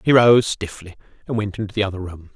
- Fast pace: Yes, fast, 230 wpm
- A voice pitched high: No, low, 100 Hz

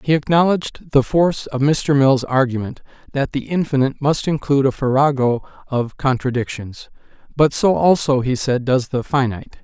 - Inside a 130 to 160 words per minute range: Yes, average, 155 wpm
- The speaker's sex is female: No, male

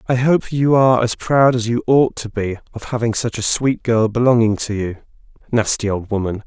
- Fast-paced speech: Yes, fast, 215 wpm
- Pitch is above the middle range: No, low, 115 Hz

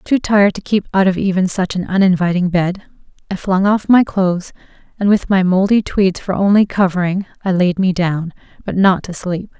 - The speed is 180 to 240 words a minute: Yes, average, 200 wpm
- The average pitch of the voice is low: No, high, 190 Hz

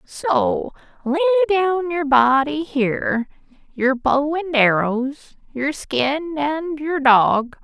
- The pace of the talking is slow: Yes, slow, 120 wpm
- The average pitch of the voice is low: No, very high, 280 Hz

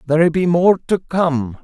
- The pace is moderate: Yes, average, 185 wpm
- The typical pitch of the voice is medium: Yes, medium, 165 Hz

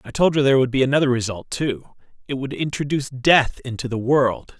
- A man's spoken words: Yes, male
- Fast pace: No, average, 195 wpm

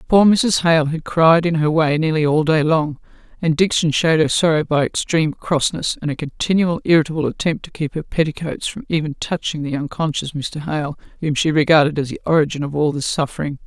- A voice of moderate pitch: Yes, medium, 155 Hz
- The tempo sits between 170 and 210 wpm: Yes, average, 200 wpm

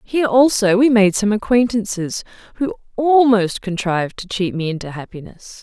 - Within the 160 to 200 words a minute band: No, average, 150 wpm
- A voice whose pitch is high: Yes, high, 210 Hz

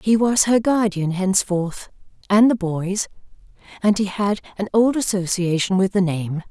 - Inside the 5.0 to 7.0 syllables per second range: No, 4.5 syllables/s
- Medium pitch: No, high, 195 Hz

